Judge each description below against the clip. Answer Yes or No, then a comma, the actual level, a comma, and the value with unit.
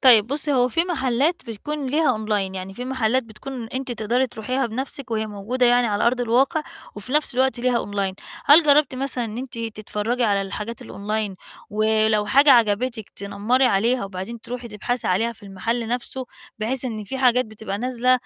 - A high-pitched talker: Yes, high, 235 Hz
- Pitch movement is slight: No, average, 3.3 semitones